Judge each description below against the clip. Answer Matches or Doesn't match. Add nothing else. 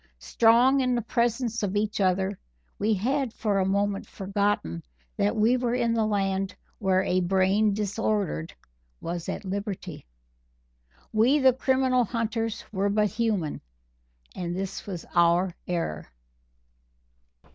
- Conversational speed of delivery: Doesn't match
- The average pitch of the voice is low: Doesn't match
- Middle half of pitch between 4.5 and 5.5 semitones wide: Doesn't match